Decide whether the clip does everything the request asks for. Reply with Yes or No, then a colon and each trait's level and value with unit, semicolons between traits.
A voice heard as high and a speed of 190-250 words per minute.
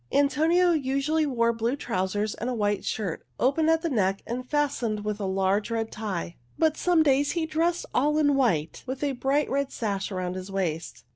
Yes: very high, 250 Hz; average, 195 wpm